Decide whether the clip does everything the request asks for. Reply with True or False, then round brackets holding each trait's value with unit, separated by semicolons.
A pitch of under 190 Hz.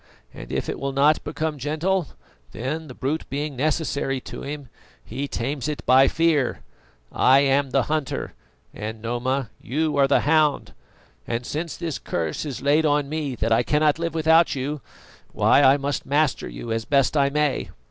True (140 Hz)